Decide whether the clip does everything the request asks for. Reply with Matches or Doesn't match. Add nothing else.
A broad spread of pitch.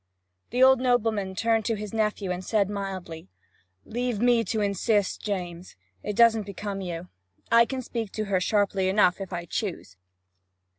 Doesn't match